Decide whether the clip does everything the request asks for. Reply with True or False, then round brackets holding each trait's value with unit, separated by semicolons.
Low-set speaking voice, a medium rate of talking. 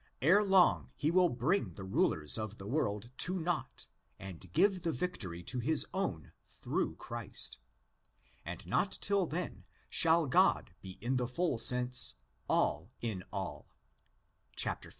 True (125 Hz; 150 wpm)